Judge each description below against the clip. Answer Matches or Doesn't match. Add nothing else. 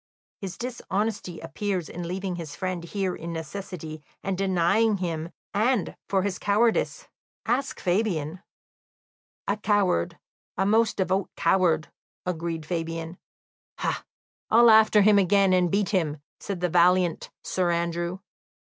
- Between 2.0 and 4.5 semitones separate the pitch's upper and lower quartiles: Matches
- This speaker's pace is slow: Matches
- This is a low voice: Doesn't match